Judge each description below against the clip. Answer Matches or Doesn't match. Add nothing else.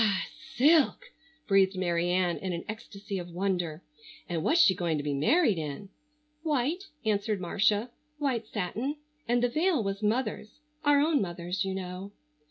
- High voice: Matches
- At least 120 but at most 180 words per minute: Matches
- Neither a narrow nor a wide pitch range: Doesn't match